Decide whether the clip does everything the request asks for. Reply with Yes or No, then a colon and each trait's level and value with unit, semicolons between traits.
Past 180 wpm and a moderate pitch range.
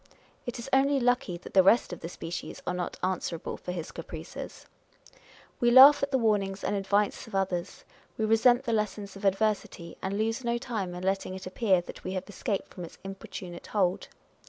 Yes: average, 195 wpm; average, 3.7 semitones